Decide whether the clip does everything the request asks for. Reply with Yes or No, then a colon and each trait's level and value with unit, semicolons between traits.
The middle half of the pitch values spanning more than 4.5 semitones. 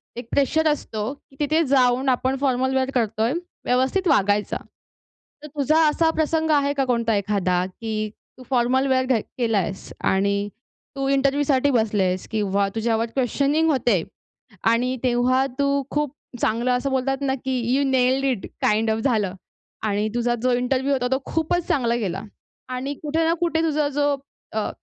No: average, 4.0 semitones